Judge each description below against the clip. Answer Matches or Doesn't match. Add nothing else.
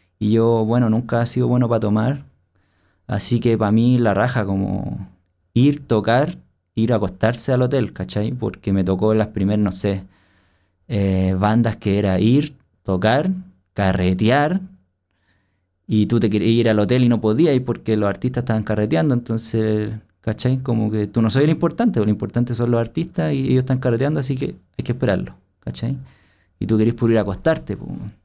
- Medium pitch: Doesn't match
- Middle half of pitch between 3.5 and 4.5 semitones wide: Matches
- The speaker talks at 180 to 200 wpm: Matches